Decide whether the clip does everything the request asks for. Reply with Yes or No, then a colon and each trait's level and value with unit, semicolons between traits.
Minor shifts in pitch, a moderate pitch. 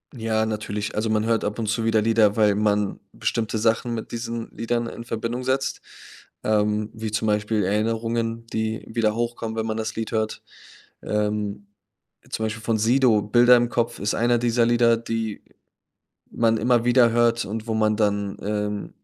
No: narrow, 1.6 semitones; low, 110 Hz